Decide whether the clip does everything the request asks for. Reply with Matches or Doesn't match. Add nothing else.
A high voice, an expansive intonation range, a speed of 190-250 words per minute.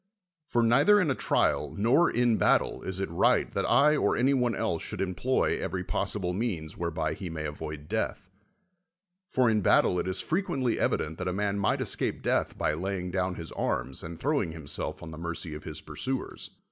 Doesn't match